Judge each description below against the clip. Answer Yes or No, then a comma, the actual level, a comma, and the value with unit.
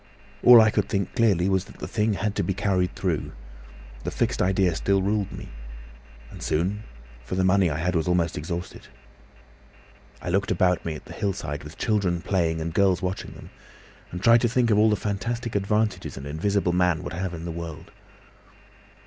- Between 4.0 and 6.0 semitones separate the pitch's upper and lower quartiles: No, average, 3.2 semitones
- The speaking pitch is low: Yes, very low, 95 Hz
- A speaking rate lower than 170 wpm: No, average, 190 wpm